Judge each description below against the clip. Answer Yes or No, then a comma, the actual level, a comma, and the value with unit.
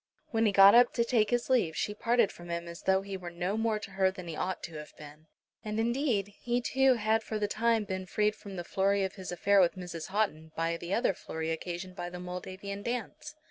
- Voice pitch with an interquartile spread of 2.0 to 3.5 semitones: No, average, 3.9 semitones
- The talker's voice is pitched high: Yes, high, 195 Hz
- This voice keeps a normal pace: No, fast, 240 wpm